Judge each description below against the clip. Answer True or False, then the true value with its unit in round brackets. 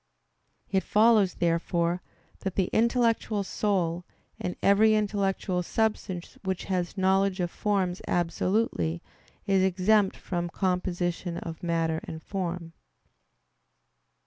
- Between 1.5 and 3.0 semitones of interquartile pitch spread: True (2.6 semitones)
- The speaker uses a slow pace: True (105 wpm)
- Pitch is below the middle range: False (185 Hz)